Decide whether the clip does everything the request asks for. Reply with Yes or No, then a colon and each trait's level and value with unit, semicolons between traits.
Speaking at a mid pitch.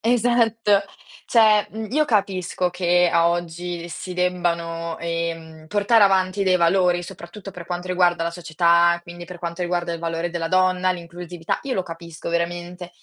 Yes: medium, 175 Hz